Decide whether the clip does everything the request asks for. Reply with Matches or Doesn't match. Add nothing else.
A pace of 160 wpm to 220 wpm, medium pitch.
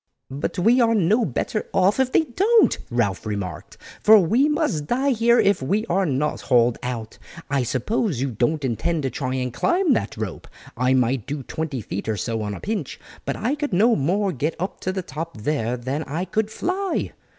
Matches